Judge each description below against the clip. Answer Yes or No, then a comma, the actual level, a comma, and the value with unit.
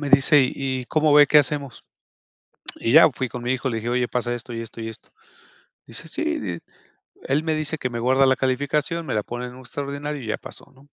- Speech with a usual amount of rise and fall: Yes, average, 3.2 semitones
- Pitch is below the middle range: Yes, low, 130 Hz